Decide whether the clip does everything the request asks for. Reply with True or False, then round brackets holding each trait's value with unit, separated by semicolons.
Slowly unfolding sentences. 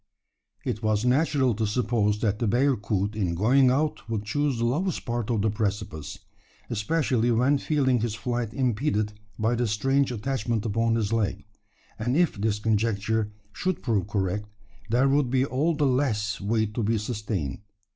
False (165 wpm)